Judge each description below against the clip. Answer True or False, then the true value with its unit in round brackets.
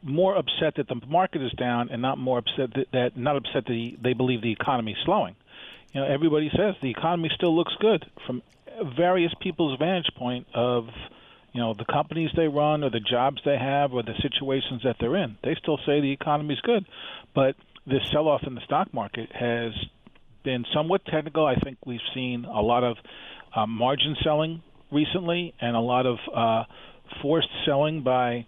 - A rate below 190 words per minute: False (195 wpm)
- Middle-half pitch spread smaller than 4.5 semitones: True (4.1 semitones)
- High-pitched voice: False (135 Hz)